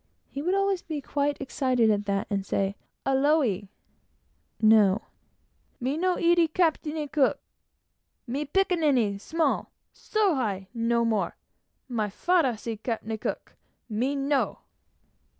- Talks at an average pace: No, slow, 120 wpm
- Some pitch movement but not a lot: No, wide, 6.3 semitones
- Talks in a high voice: Yes, very high, 265 Hz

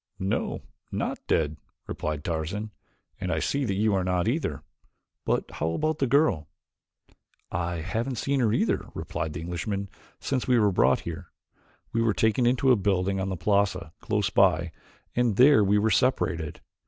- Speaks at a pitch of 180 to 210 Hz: No, low, 100 Hz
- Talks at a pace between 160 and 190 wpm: Yes, average, 165 wpm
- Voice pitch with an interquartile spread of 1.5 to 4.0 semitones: No, wide, 5.6 semitones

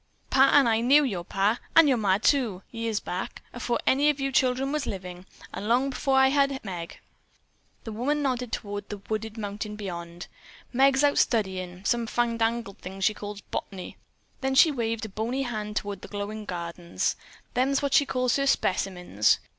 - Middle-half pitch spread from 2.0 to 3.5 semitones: No, average, 5.0 semitones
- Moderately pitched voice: No, high, 225 Hz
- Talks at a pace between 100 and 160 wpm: No, average, 180 wpm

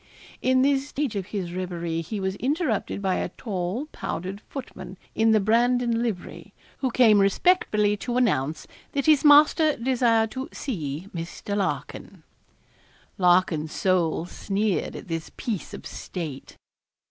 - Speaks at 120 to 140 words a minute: Yes, slow, 135 wpm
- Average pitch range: No, wide, 5.8 semitones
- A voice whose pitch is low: No, high, 210 Hz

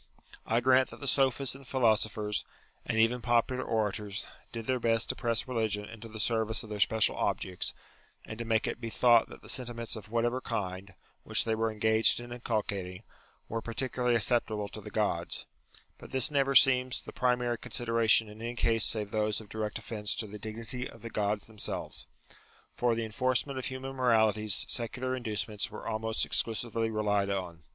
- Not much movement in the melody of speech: Yes, narrow, 2.3 semitones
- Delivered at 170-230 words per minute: Yes, average, 180 wpm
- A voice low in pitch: Yes, low, 115 Hz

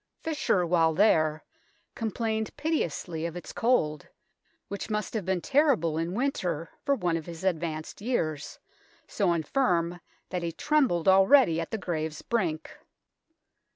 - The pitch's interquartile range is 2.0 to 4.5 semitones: No, average, 5.3 semitones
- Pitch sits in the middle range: Yes, medium, 175 Hz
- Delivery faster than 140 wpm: No, slow, 135 wpm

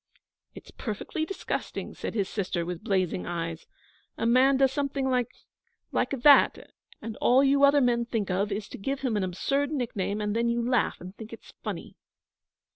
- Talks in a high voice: Yes, high, 235 Hz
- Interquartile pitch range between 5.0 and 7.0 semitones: Yes, average, 5.3 semitones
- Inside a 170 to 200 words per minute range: Yes, average, 180 wpm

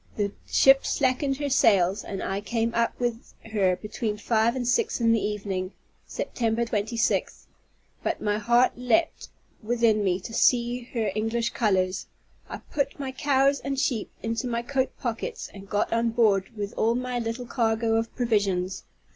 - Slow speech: No, average, 165 wpm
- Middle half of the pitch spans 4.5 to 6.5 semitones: No, average, 2.9 semitones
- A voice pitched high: Yes, high, 230 Hz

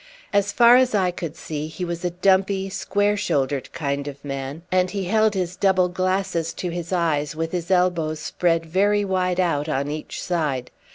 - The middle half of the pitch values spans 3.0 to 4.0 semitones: Yes, average, 3.6 semitones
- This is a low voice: No, medium, 180 Hz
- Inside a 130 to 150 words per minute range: No, average, 185 wpm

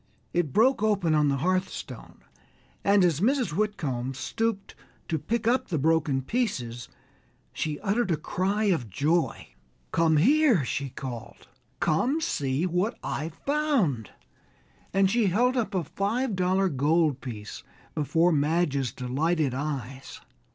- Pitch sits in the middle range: Yes, medium, 165 Hz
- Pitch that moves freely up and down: Yes, wide, 6.7 semitones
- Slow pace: Yes, slow, 130 wpm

